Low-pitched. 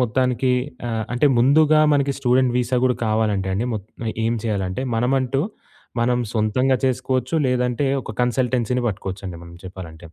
Yes: low, 125 Hz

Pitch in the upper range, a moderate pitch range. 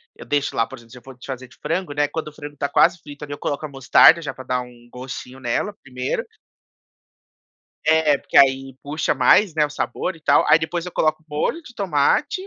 No: medium, 145 Hz; average, 3.4 semitones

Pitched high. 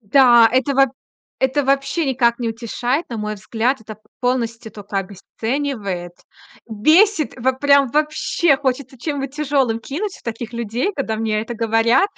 Yes: very high, 250 Hz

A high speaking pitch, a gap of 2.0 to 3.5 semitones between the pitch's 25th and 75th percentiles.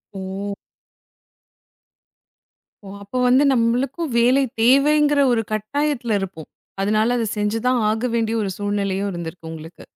No: high, 225 Hz; average, 4.2 semitones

